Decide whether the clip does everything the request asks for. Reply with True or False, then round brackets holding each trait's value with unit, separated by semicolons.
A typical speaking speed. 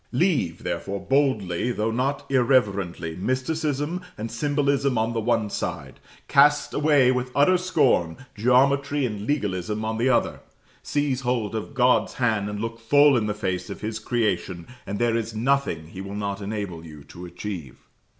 True (160 wpm)